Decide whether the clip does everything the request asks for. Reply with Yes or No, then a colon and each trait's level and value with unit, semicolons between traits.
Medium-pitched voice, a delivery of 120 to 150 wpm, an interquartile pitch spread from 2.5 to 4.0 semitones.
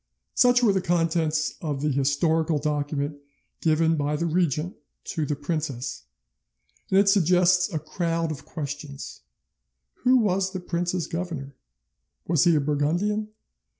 Yes: medium, 165 Hz; average, 140 wpm; average, 3.4 semitones